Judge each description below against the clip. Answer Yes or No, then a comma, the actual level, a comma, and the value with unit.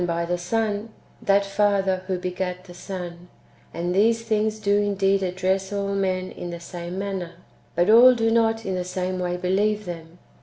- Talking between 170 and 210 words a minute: Yes, average, 180 wpm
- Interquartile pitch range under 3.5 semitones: Yes, narrow, 2.4 semitones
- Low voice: No, high, 190 Hz